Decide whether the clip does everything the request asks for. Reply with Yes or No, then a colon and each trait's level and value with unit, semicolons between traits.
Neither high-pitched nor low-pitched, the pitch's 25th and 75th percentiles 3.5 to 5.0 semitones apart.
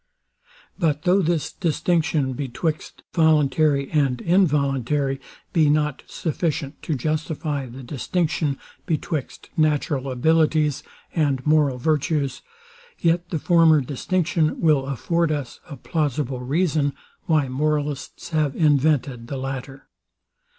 No: medium, 150 Hz; narrow, 2.6 semitones